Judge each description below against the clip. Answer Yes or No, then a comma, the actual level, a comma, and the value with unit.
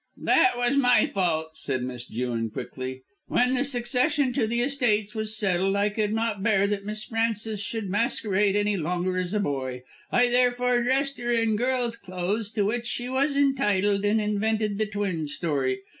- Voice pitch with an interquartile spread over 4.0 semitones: Yes, average, 4.4 semitones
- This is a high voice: Yes, high, 210 Hz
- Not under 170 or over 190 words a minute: Yes, average, 175 wpm